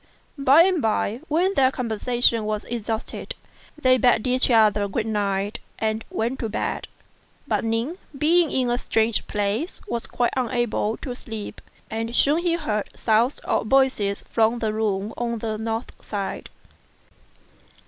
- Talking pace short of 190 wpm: Yes, average, 150 wpm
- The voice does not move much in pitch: No, average, 3.0 semitones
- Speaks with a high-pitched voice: Yes, high, 230 Hz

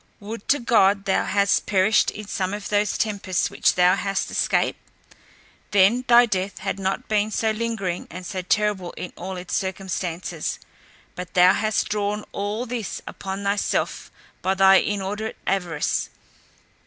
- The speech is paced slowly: No, average, 150 wpm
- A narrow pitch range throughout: Yes, narrow, 2.0 semitones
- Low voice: No, high, 200 Hz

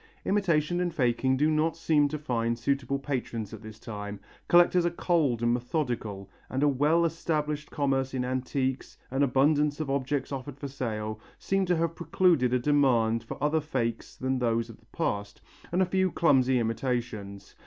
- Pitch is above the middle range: No, low, 135 Hz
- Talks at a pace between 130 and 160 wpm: No, average, 175 wpm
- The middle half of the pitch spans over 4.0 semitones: Yes, average, 4.5 semitones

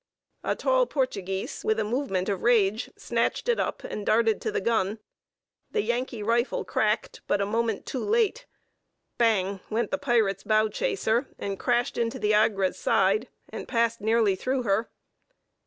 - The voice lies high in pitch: Yes, high, 225 Hz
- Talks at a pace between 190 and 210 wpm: No, average, 160 wpm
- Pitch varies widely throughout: No, average, 3.2 semitones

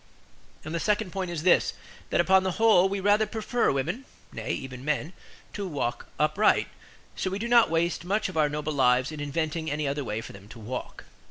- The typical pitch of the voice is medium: Yes, medium, 165 Hz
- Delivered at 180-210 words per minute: Yes, fast, 205 wpm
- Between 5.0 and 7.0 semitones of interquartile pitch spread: Yes, average, 5.3 semitones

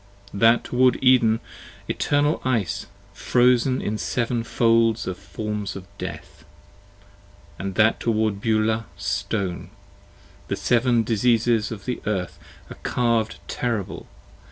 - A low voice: Yes, low, 115 Hz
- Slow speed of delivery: Yes, slow, 115 wpm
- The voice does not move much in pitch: Yes, narrow, 2.2 semitones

